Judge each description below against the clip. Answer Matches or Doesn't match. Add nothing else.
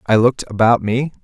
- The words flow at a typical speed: Matches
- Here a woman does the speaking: Doesn't match